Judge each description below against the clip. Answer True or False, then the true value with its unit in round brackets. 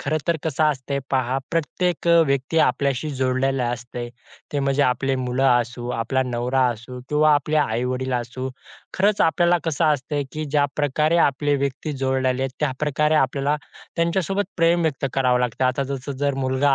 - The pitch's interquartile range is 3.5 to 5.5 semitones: False (3.1 semitones)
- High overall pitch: False (135 Hz)